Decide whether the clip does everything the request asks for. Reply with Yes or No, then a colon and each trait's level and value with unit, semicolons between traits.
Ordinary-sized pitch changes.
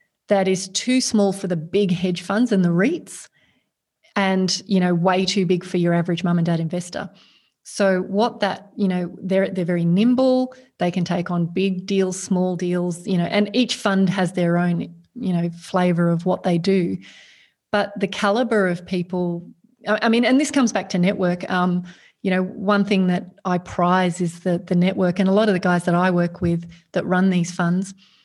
No: narrow, 2.2 semitones